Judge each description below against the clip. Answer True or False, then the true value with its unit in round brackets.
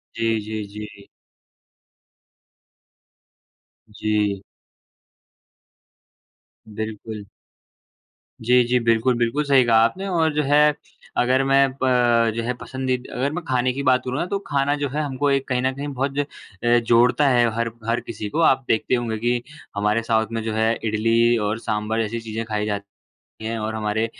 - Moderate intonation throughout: True (3.1 semitones)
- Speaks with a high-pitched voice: False (120 Hz)